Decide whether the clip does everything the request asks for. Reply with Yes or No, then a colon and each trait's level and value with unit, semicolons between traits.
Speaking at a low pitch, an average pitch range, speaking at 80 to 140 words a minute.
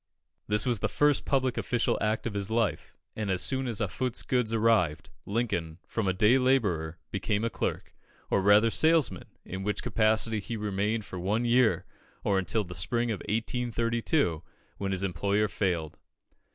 No: low, 110 Hz; average, 3.3 semitones; average, 165 wpm